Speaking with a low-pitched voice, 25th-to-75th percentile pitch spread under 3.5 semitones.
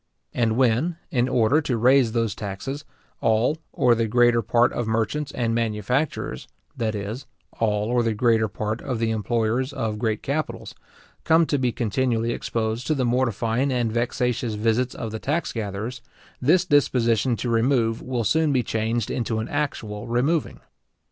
Yes: low, 120 Hz; average, 2.7 semitones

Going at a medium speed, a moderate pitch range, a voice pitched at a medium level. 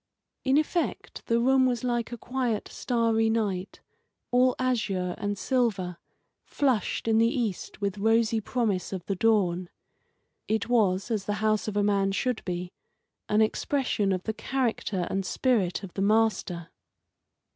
No: average, 150 wpm; average, 3.6 semitones; high, 220 Hz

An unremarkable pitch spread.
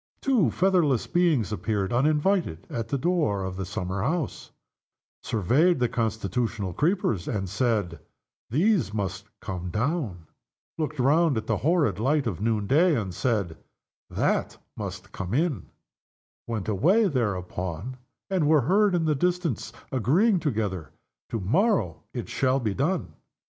No: wide, 8.2 semitones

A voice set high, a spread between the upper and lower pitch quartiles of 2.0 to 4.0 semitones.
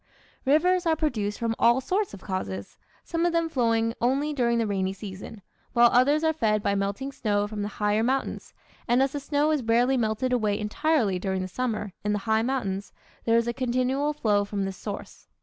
No: high, 230 Hz; average, 4.8 semitones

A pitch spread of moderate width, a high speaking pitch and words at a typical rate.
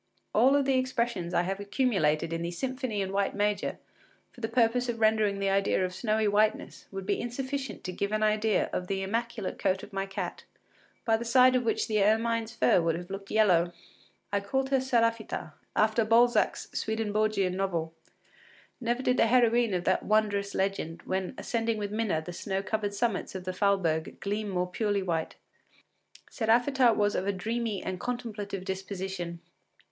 Yes: average, 3.3 semitones; high, 210 Hz; average, 175 wpm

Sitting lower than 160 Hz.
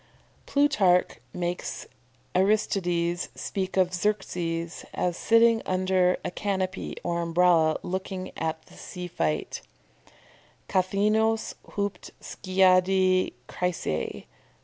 No: medium, 185 Hz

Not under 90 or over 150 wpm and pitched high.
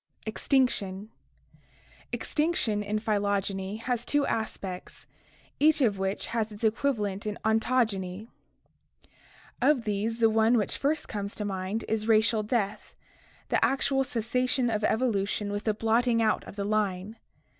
Yes: average, 145 wpm; high, 220 Hz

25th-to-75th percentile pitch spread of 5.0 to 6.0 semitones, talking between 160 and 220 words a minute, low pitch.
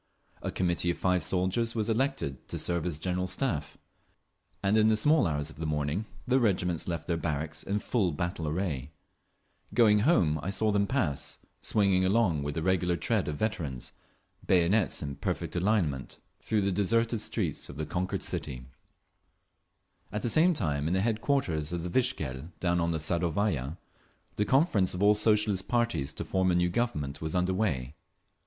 Yes: average, 5.3 semitones; average, 175 wpm; very low, 90 Hz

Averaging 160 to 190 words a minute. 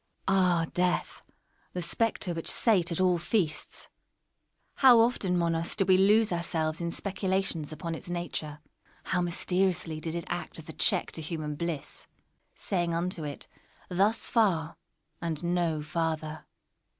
No: average, 140 wpm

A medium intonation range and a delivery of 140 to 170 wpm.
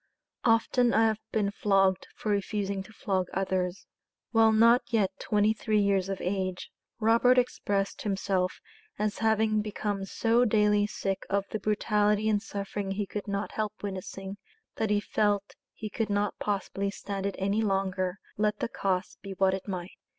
No: narrow, 1.8 semitones; average, 165 wpm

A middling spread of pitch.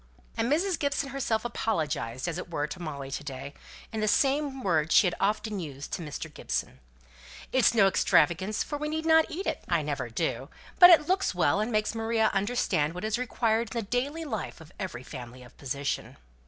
No: wide, 8.7 semitones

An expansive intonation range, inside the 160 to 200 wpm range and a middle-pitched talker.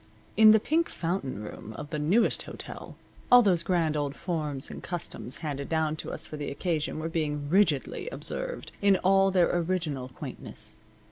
No: average, 4.5 semitones; average, 175 wpm; medium, 165 Hz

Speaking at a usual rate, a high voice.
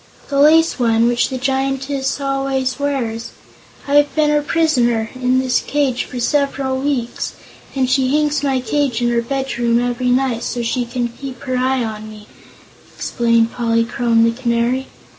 Yes: average, 165 wpm; very high, 255 Hz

